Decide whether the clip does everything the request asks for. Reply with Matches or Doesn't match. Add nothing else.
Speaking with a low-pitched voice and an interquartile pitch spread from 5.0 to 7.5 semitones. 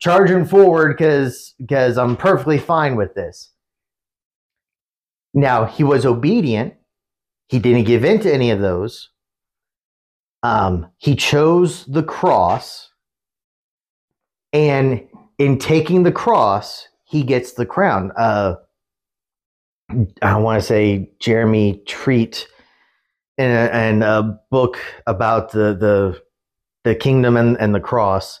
Matches